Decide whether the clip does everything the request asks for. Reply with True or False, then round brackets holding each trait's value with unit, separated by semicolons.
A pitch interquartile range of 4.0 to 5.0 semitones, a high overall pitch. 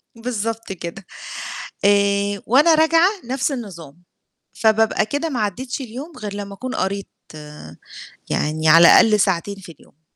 True (4.6 semitones; 210 Hz)